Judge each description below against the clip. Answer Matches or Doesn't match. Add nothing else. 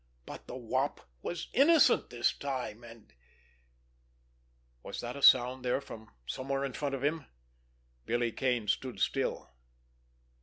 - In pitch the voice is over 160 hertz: Doesn't match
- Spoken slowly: Matches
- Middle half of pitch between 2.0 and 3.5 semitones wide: Matches